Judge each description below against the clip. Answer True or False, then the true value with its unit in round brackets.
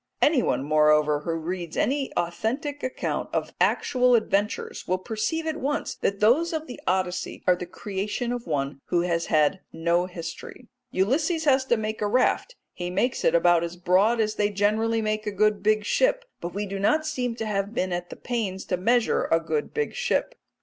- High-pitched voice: True (210 Hz)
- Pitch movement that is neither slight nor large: False (5.8 semitones)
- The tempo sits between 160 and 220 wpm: True (190 wpm)